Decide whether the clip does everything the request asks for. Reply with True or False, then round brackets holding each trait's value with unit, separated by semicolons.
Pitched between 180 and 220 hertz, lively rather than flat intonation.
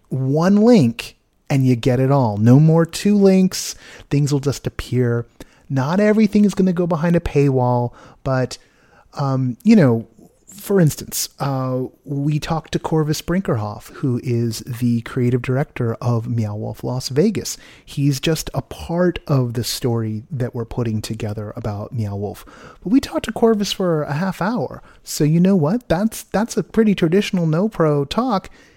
False (140 Hz; 6.9 semitones)